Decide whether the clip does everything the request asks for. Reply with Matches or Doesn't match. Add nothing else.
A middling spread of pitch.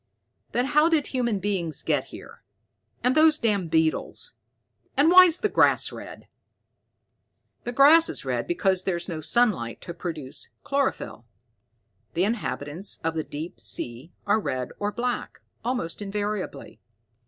Doesn't match